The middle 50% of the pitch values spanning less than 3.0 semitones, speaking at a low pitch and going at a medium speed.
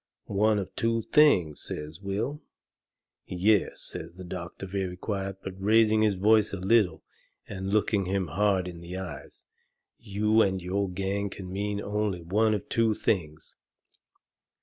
Yes: narrow, 2.6 semitones; low, 100 Hz; average, 150 wpm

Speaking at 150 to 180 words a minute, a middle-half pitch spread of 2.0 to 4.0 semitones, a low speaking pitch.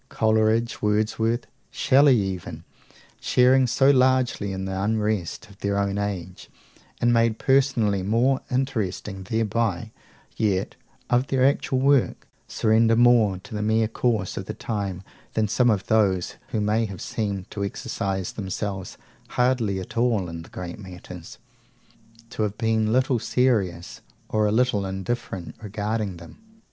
No: slow, 135 wpm; average, 3.5 semitones; low, 110 Hz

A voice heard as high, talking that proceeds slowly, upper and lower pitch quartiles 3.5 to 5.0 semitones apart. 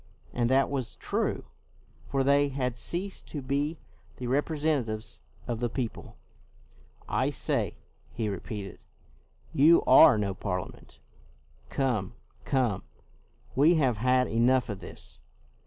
No: low, 130 Hz; slow, 125 wpm; average, 4.0 semitones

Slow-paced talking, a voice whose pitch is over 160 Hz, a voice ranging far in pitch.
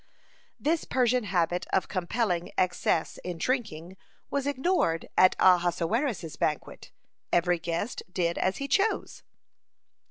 Yes: slow, 115 wpm; medium, 185 Hz; wide, 6.6 semitones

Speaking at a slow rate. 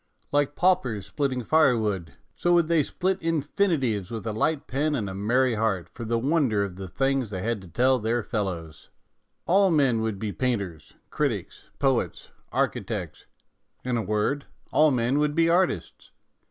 No: average, 165 wpm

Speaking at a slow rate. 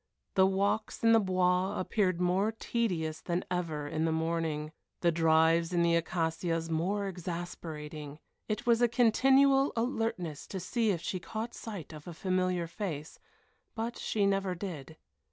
No: average, 155 wpm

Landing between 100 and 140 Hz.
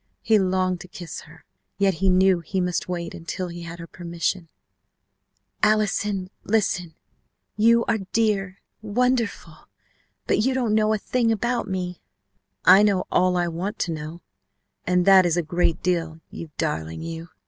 No: medium, 185 Hz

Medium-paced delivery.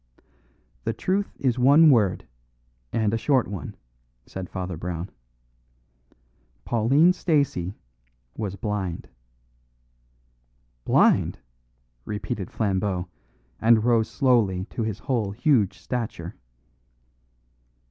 No: slow, 90 wpm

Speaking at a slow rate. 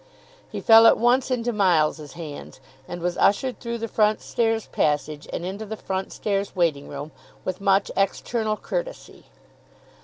No: average, 155 wpm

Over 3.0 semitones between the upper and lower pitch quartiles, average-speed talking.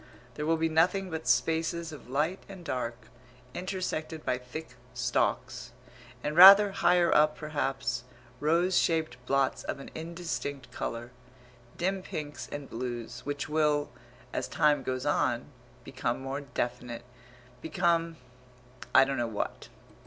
No: average, 4.6 semitones; slow, 130 wpm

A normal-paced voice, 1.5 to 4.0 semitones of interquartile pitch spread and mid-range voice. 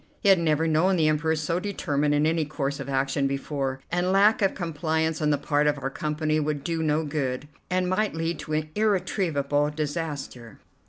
Yes: average, 190 wpm; narrow, 2.6 semitones; medium, 155 Hz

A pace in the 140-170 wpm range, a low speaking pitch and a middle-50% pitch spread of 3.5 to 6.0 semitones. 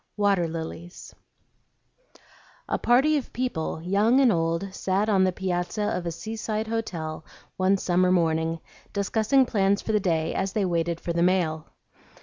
No: average, 150 wpm; high, 190 Hz; average, 4.1 semitones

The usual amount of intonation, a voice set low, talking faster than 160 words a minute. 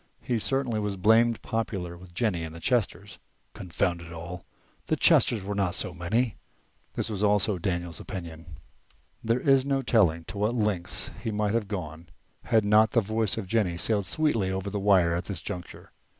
Yes: average, 4.2 semitones; low, 100 Hz; average, 180 wpm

